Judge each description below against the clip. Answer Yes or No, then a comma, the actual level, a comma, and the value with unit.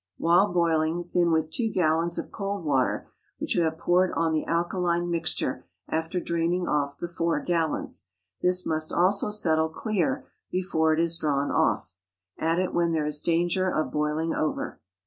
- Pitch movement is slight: Yes, narrow, 2.0 semitones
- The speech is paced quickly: No, average, 165 wpm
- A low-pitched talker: No, medium, 170 Hz